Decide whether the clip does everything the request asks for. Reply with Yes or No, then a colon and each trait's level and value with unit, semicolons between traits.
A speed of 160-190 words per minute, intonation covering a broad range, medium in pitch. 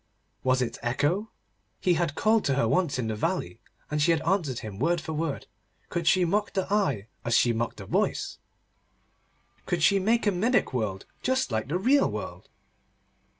Yes: average, 185 wpm; wide, 7.3 semitones; medium, 165 Hz